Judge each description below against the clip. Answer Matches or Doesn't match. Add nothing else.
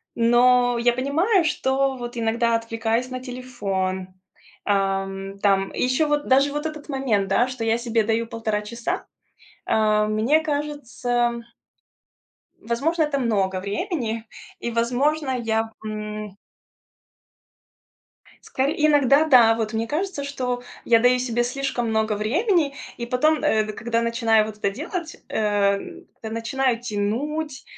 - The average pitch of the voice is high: Matches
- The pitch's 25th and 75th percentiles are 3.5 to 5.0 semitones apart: Matches